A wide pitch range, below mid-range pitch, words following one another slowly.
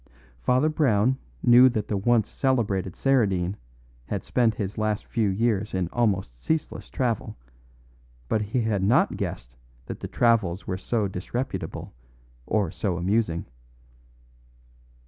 No: average, 4.0 semitones; low, 105 Hz; slow, 125 wpm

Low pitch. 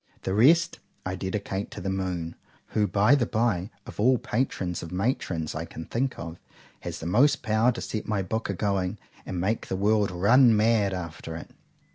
Yes: low, 100 Hz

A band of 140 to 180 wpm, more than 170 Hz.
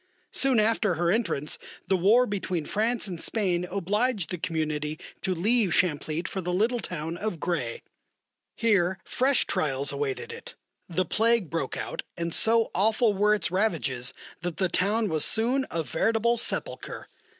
Yes: average, 155 wpm; medium, 185 Hz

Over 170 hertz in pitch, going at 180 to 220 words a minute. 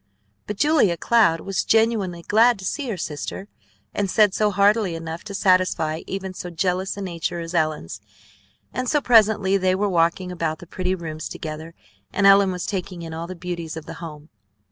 Yes: medium, 185 Hz; average, 190 wpm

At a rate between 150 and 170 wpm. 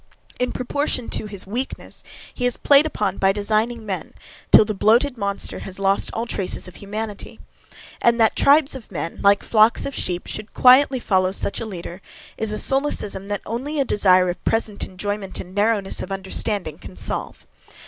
No: average, 180 wpm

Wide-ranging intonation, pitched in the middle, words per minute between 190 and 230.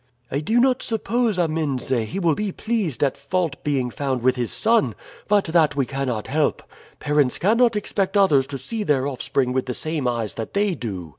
Yes: wide, 7.4 semitones; medium, 150 Hz; average, 195 wpm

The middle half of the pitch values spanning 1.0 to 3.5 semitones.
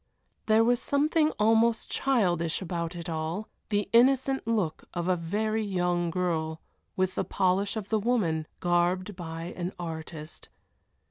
No: average, 4.6 semitones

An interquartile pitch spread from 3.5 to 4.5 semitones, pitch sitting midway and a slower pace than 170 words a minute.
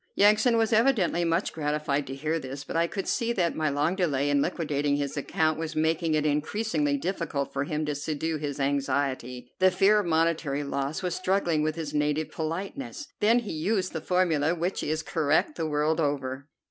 No: average, 3.8 semitones; medium, 155 Hz; average, 190 wpm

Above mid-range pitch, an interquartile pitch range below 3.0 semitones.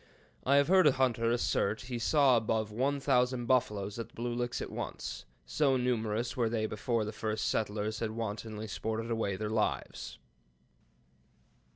No: low, 115 Hz; narrow, 2.5 semitones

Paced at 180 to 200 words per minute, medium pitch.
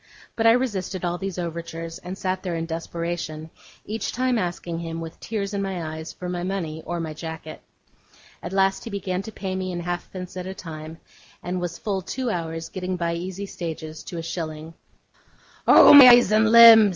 Yes: average, 195 wpm; medium, 180 Hz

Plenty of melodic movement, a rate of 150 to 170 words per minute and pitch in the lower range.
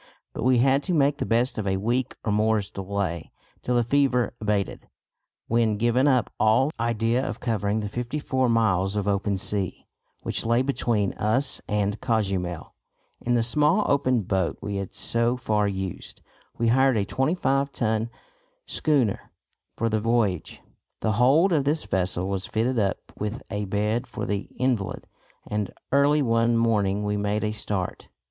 No: average, 3.7 semitones; average, 165 wpm; low, 115 Hz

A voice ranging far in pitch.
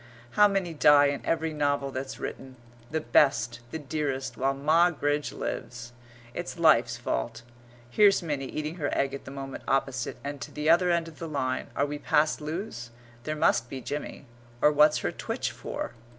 No: average, 2.9 semitones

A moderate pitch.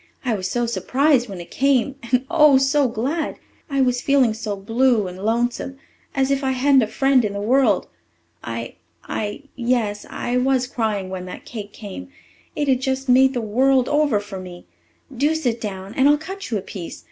No: high, 245 Hz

